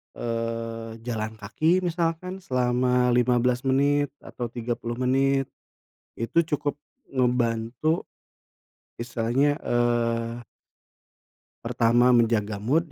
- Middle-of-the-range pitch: No, low, 125 Hz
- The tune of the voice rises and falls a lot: No, average, 2.9 semitones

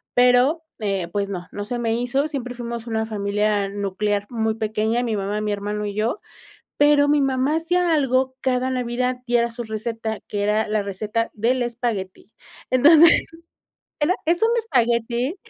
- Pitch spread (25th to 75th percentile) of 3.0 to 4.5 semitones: Yes, average, 3.6 semitones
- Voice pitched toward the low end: No, high, 235 Hz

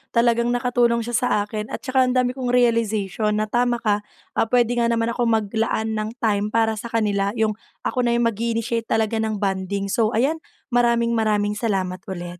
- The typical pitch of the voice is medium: No, high, 225 Hz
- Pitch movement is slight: Yes, narrow, 2.1 semitones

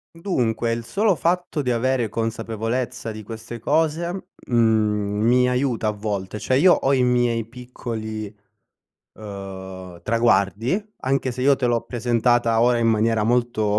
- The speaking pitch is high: No, low, 115 Hz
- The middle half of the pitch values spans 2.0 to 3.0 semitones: Yes, average, 2.7 semitones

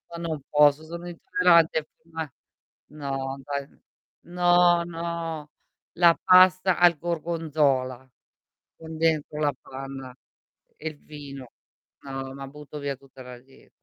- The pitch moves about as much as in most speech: Yes, average, 3.6 semitones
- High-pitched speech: No, medium, 155 Hz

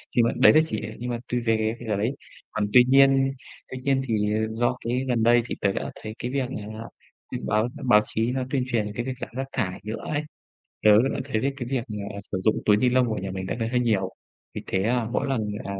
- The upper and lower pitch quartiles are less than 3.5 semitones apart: Yes, average, 3.1 semitones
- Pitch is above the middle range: No, low, 120 Hz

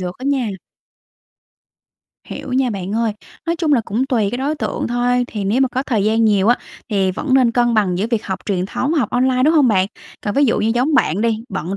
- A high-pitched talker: Yes, high, 235 Hz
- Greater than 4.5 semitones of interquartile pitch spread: No, average, 4.2 semitones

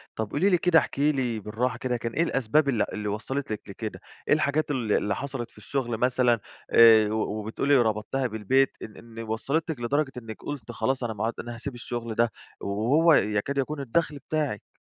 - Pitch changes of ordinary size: Yes, average, 4.1 semitones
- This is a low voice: Yes, low, 120 Hz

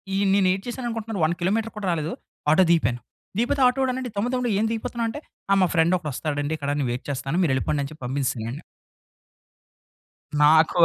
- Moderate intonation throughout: No, wide, 7.7 semitones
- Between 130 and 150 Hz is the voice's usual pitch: No, medium, 175 Hz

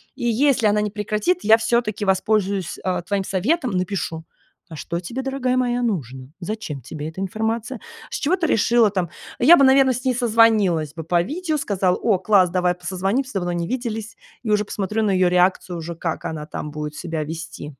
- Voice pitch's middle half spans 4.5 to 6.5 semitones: Yes, average, 5.2 semitones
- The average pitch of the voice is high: Yes, high, 200 Hz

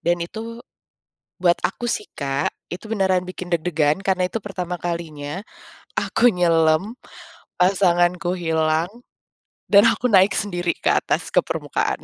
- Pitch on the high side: No, medium, 180 Hz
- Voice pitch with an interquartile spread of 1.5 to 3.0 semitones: Yes, narrow, 2.6 semitones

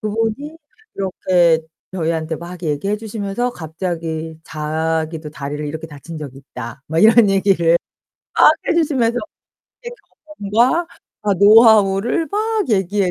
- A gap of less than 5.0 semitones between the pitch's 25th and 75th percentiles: No, wide, 5.6 semitones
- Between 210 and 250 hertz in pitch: No, medium, 185 Hz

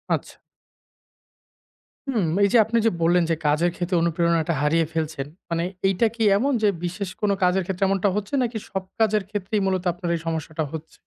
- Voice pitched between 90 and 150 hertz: No, medium, 180 Hz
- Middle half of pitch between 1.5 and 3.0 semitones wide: No, average, 3.6 semitones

